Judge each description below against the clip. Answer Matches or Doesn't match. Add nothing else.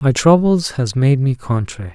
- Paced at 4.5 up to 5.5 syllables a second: Matches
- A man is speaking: Matches